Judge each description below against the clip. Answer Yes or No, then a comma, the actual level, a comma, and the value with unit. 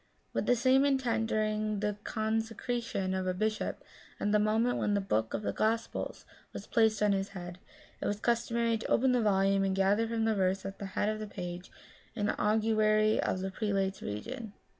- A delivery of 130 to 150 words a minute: No, average, 195 wpm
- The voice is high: Yes, high, 215 Hz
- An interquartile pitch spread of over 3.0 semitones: No, narrow, 2.4 semitones